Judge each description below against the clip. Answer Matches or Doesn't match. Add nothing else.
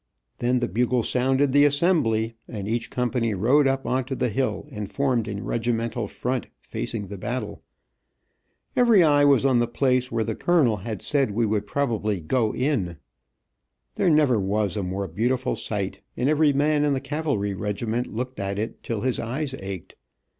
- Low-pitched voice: Matches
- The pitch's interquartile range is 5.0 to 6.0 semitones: Doesn't match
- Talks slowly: Doesn't match